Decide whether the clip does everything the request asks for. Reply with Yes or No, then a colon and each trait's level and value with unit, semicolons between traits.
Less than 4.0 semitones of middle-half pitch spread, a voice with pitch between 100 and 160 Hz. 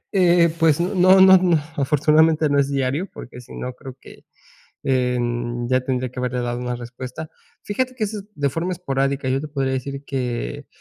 No: average, 4.9 semitones; medium, 140 Hz